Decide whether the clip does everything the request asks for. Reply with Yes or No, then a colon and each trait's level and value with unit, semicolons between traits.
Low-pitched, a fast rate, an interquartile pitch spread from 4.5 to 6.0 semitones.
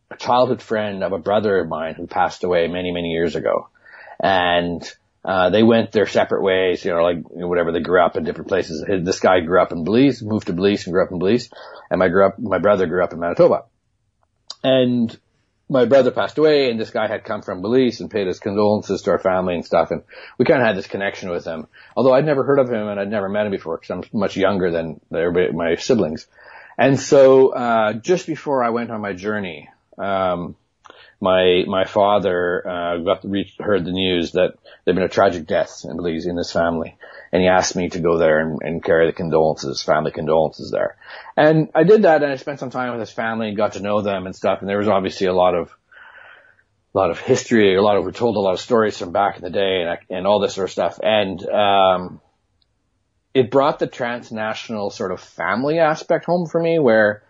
Yes: low, 105 Hz; fast, 230 wpm; average, 5.3 semitones